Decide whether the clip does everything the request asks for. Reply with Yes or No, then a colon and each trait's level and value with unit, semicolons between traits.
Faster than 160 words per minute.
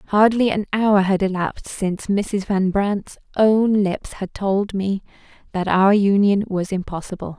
No: average, 155 wpm